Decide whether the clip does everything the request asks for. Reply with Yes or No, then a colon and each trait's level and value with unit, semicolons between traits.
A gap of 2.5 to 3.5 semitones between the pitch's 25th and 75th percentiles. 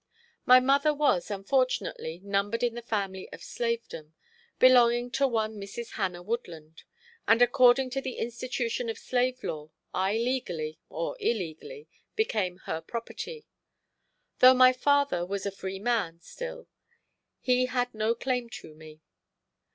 No: average, 4.8 semitones